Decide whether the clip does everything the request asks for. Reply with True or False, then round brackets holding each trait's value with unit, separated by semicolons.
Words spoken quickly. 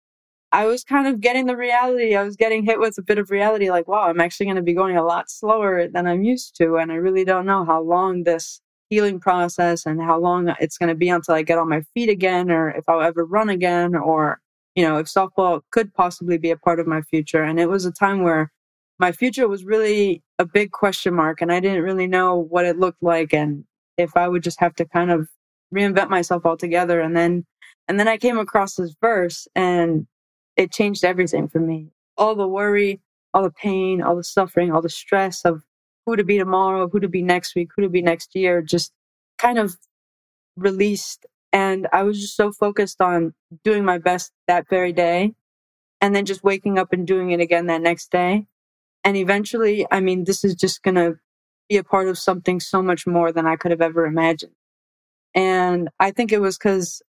True (220 wpm)